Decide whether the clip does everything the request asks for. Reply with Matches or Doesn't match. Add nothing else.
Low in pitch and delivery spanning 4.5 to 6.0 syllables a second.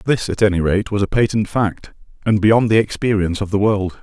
Matches